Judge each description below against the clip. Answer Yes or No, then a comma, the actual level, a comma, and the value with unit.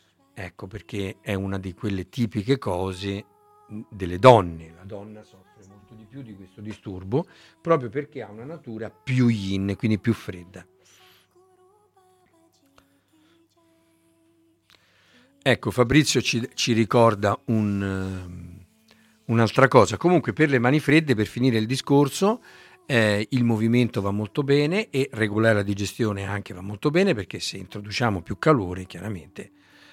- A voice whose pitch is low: Yes, low, 115 Hz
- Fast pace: No, average, 135 wpm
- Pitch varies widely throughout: Yes, wide, 6.1 semitones